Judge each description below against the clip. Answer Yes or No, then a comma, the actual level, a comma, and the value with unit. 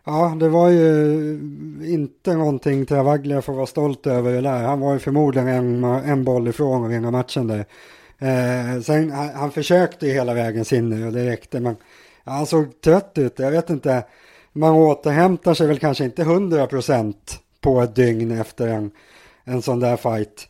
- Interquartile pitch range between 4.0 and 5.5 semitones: No, average, 3.6 semitones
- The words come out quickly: No, average, 185 wpm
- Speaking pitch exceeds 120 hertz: Yes, low, 135 Hz